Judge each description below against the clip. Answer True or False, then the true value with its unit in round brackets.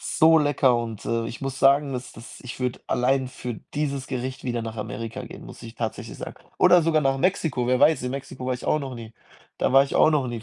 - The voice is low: True (130 Hz)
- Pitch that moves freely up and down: False (2.5 semitones)